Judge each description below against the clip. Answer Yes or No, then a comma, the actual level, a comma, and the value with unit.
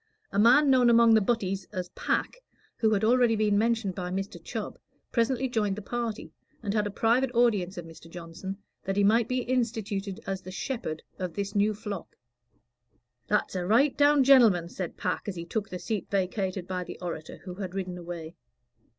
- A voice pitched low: No, high, 205 Hz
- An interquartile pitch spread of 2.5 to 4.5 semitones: Yes, average, 4.0 semitones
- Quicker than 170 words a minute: Yes, average, 190 wpm